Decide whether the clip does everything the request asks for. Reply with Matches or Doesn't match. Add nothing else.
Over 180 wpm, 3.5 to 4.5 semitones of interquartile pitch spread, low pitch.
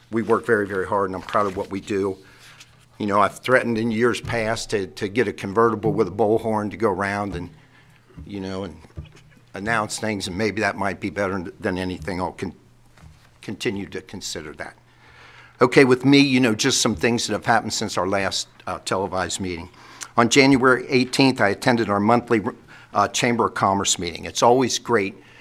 Matches